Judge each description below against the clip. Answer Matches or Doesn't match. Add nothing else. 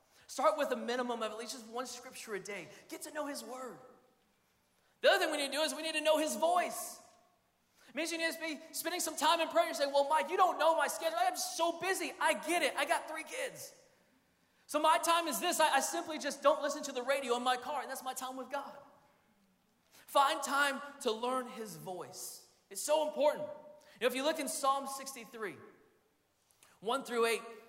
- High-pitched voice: Matches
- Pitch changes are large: Doesn't match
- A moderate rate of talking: Doesn't match